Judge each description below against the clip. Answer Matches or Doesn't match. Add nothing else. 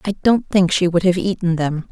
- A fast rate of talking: Matches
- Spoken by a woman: Matches